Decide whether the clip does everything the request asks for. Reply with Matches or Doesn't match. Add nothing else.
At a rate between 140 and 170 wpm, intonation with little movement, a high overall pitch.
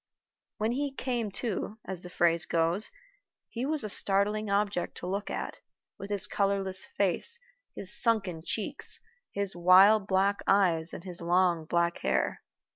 Doesn't match